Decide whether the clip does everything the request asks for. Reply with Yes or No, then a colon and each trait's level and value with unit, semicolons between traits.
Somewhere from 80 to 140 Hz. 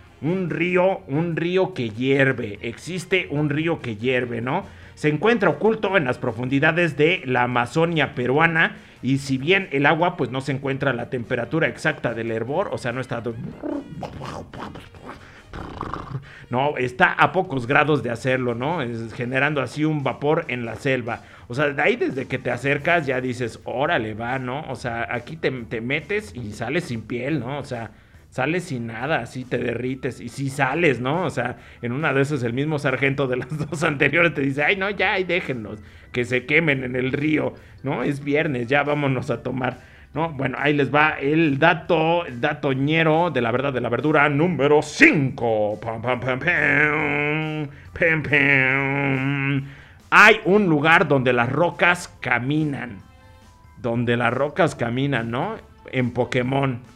Yes: low, 135 Hz